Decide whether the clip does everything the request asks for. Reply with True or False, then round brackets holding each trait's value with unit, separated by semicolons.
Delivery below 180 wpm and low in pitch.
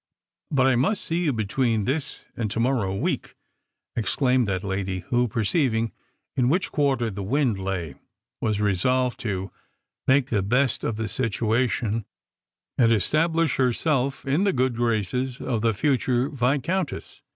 True (155 wpm; 120 Hz)